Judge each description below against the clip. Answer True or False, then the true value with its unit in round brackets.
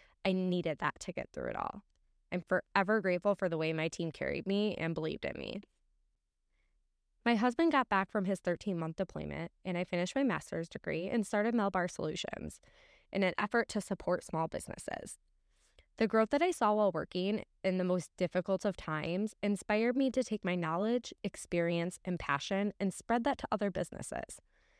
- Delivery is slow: False (185 wpm)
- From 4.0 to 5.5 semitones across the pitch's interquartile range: False (3.4 semitones)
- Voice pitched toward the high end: True (195 Hz)